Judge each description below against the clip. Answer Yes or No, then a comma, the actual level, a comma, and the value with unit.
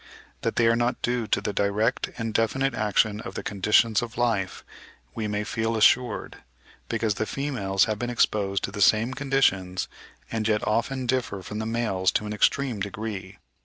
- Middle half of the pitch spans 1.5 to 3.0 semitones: Yes, average, 2.7 semitones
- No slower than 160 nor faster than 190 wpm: Yes, average, 180 wpm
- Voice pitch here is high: No, low, 110 Hz